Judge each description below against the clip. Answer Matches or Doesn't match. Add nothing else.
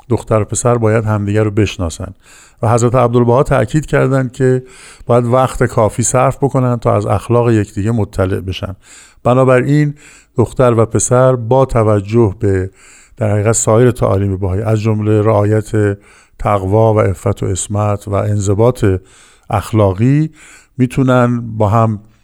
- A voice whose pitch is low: Matches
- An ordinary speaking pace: Matches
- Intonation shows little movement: Doesn't match